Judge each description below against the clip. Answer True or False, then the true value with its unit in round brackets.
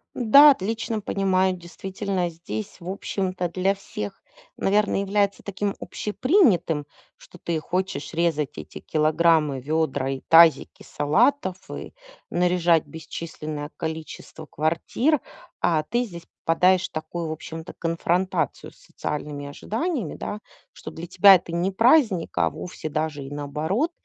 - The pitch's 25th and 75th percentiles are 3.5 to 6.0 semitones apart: True (4.0 semitones)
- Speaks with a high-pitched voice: False (175 Hz)